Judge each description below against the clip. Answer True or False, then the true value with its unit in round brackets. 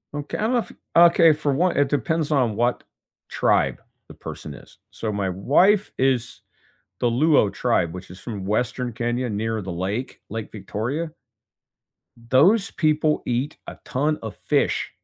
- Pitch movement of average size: False (6.0 semitones)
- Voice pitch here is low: True (125 Hz)